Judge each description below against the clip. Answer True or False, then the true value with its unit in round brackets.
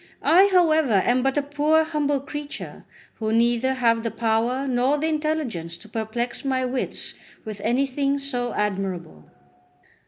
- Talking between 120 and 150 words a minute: True (145 wpm)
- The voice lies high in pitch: True (255 Hz)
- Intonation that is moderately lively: True (4.3 semitones)